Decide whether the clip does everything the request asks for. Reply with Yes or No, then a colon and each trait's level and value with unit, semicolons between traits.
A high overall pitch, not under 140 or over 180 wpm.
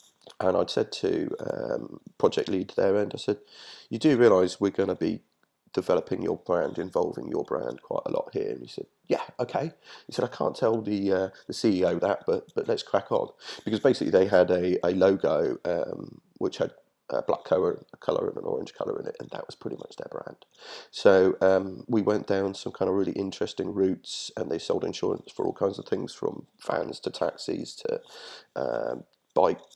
No: very high, 400 Hz; fast, 205 wpm